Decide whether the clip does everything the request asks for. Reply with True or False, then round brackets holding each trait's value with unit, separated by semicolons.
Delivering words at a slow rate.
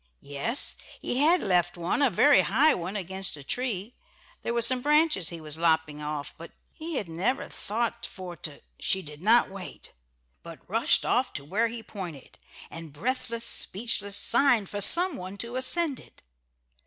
False (175 wpm)